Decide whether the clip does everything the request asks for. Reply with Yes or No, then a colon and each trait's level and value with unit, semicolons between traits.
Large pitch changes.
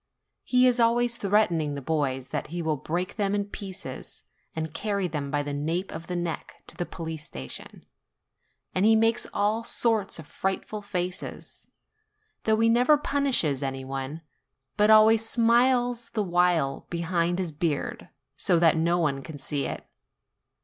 Yes: wide, 5.8 semitones